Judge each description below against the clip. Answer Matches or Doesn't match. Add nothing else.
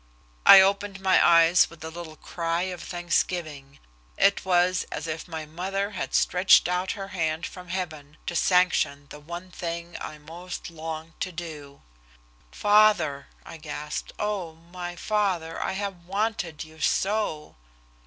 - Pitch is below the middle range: Doesn't match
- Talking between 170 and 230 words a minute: Doesn't match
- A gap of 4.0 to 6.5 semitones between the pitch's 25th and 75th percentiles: Doesn't match